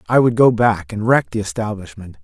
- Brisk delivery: Yes, fast, 215 wpm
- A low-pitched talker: Yes, low, 105 Hz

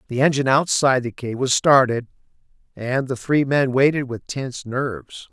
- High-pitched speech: No, low, 130 Hz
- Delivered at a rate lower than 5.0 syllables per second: No, 5.2 syllables/s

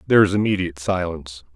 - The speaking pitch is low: Yes, very low, 90 Hz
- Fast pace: No, average, 155 wpm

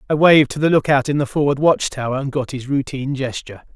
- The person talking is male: Yes, male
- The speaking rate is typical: No, fast, 240 wpm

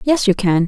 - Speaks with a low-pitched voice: No, high, 210 Hz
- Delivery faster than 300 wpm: No, fast, 265 wpm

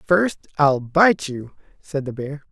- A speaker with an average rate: Yes, average, 165 wpm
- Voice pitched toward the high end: No, medium, 150 Hz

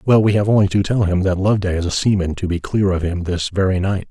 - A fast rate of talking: Yes, fast, 295 wpm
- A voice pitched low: Yes, very low, 95 Hz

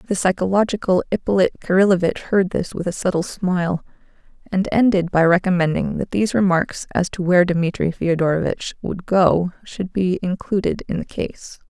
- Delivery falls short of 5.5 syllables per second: Yes, 5.1 syllables/s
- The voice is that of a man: No, female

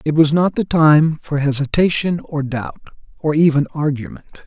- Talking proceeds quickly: No, average, 160 wpm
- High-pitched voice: No, medium, 150 Hz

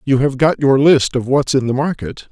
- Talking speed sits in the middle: No, fast, 260 wpm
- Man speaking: Yes, male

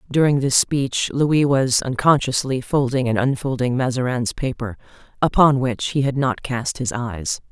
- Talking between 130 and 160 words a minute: Yes, average, 150 wpm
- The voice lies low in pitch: Yes, low, 130 Hz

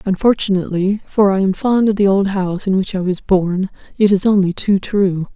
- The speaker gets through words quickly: Yes, fast, 215 wpm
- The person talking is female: Yes, female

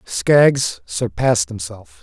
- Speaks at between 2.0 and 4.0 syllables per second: Yes, 3.2 syllables/s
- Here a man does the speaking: Yes, male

